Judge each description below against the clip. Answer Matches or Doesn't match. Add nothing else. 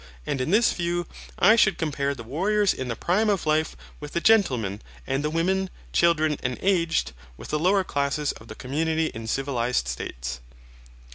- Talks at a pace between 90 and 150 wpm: Doesn't match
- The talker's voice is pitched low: Doesn't match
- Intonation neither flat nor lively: Doesn't match